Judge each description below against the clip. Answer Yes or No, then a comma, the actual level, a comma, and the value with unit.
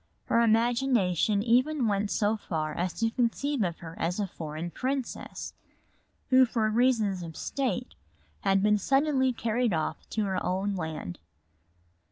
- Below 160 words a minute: Yes, average, 145 wpm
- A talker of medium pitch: No, high, 215 Hz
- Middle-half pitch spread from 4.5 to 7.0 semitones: Yes, wide, 5.4 semitones